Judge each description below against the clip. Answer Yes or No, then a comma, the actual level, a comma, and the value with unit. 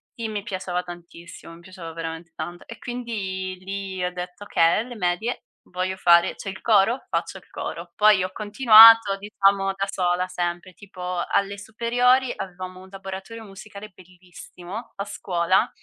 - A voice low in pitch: No, high, 190 Hz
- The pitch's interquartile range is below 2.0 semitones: No, average, 2.8 semitones